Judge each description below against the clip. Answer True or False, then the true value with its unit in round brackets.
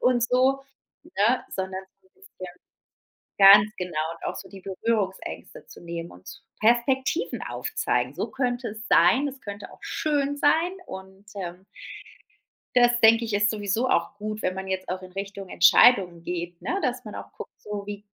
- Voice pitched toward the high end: True (205 Hz)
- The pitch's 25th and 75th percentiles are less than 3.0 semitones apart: False (4.7 semitones)